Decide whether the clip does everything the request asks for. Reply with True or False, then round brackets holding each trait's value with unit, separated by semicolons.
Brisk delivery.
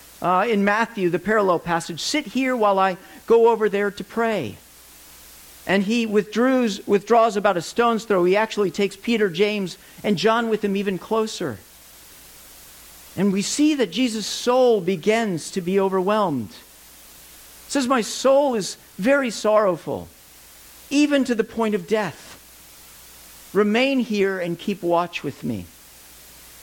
False (140 wpm)